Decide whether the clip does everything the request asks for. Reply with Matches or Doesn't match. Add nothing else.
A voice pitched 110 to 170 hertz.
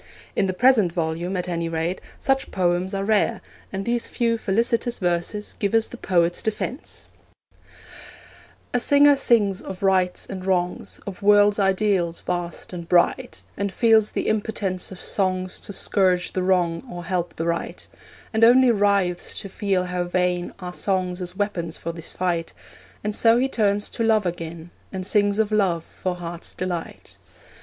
Doesn't match